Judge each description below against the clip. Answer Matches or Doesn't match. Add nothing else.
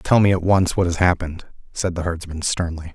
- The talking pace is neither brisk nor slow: Doesn't match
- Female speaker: Doesn't match